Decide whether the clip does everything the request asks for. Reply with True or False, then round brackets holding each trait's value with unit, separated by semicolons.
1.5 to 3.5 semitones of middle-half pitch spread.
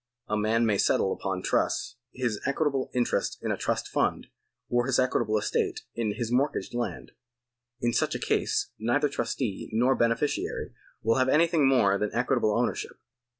True (3.2 semitones)